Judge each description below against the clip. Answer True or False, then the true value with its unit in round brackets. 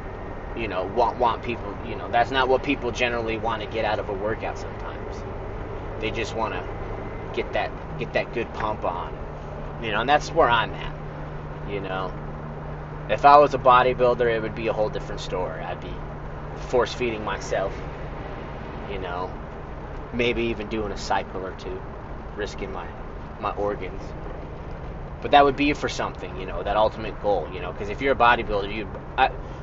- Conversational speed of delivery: True (180 wpm)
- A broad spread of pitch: True (6.7 semitones)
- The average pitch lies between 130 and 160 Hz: False (100 Hz)